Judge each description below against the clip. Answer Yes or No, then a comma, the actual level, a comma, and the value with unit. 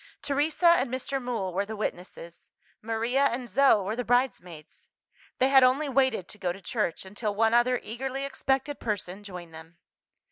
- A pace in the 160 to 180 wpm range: Yes, average, 170 wpm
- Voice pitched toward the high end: Yes, high, 235 Hz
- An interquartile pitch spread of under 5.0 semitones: No, wide, 5.5 semitones